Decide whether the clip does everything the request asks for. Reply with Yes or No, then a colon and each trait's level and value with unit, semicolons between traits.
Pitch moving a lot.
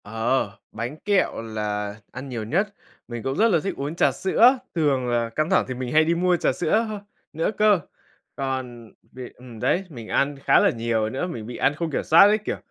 Yes: wide, 6.4 semitones